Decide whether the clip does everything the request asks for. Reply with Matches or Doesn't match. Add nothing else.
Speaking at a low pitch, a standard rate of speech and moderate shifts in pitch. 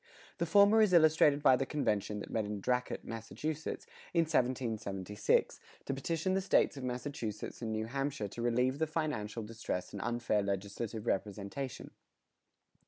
Doesn't match